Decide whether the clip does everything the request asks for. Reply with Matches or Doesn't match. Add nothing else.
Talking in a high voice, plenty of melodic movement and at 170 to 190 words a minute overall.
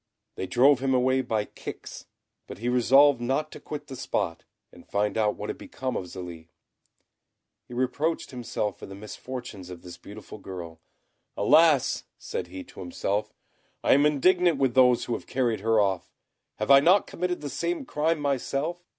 Doesn't match